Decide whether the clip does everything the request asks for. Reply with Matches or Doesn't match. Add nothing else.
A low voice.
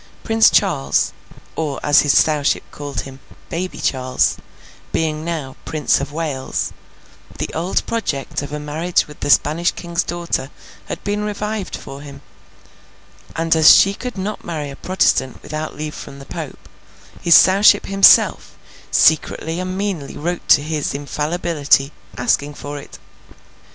Doesn't match